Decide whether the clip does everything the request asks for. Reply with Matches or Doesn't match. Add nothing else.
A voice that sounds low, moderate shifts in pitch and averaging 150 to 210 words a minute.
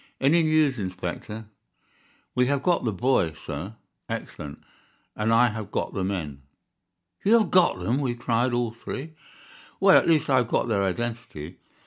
Doesn't match